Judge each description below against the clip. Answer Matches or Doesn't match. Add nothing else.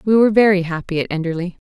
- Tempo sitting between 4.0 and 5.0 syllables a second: Doesn't match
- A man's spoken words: Doesn't match